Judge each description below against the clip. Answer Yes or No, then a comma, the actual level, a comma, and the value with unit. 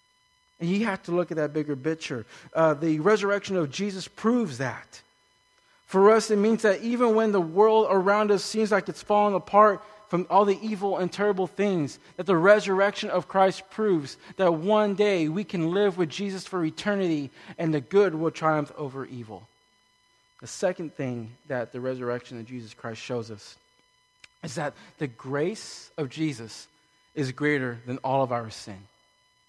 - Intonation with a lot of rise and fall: Yes, wide, 7.0 semitones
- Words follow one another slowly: No, average, 175 wpm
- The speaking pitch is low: No, medium, 175 Hz